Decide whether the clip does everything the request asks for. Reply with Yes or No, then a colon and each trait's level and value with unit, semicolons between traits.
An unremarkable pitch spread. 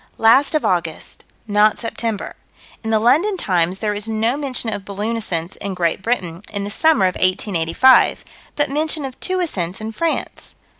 No: wide, 5.7 semitones